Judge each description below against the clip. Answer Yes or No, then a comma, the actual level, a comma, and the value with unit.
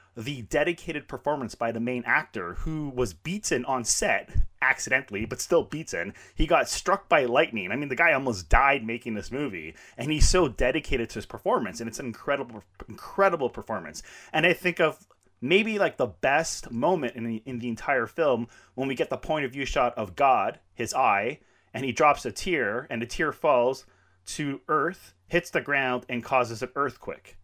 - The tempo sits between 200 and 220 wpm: No, average, 190 wpm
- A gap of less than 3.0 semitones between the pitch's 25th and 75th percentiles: No, average, 4.4 semitones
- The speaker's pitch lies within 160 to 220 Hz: No, low, 125 Hz